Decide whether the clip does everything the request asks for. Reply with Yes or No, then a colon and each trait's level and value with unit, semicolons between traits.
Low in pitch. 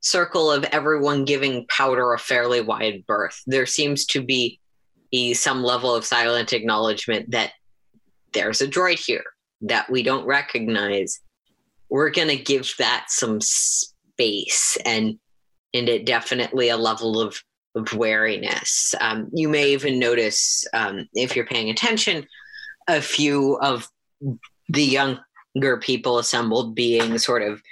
Yes: low, 125 Hz